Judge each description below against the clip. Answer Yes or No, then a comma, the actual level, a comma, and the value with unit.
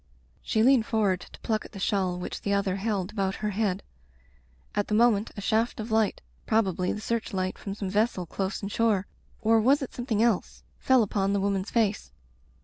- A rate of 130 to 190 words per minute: No, fast, 205 wpm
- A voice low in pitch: No, high, 210 Hz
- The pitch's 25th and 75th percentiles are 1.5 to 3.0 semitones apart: Yes, narrow, 2.5 semitones